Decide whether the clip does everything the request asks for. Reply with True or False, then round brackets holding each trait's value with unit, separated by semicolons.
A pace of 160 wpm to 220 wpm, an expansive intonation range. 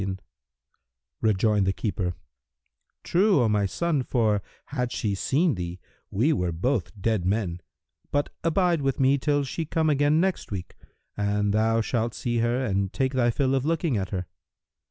True (165 wpm; 6.2 semitones)